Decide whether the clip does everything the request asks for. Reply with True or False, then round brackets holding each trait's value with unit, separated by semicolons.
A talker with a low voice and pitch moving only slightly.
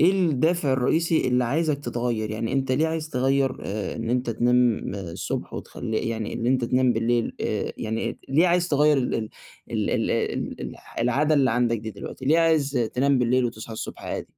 False (125 Hz; 4.2 semitones)